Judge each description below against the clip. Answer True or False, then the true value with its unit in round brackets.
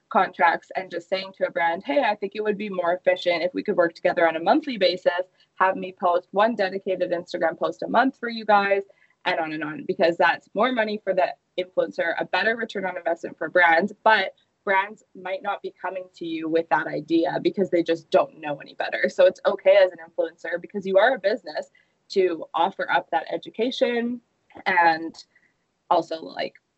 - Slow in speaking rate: False (205 wpm)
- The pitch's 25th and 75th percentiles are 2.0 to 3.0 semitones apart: False (3.6 semitones)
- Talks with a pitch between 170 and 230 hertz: True (185 Hz)